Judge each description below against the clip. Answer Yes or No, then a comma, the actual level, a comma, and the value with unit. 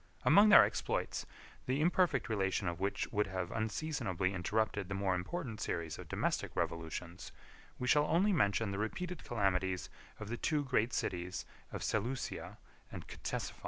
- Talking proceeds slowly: No, average, 155 wpm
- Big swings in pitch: Yes, wide, 6.1 semitones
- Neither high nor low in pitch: No, low, 105 Hz